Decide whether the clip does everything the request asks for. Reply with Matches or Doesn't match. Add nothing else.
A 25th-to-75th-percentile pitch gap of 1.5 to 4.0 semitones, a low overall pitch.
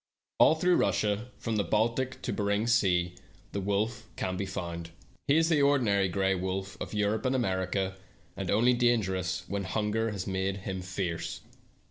Matches